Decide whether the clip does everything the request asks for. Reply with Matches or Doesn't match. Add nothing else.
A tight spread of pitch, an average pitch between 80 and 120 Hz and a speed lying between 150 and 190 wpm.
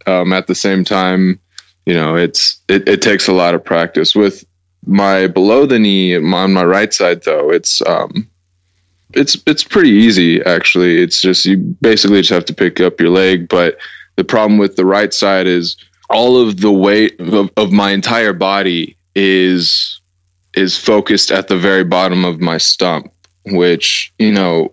Matches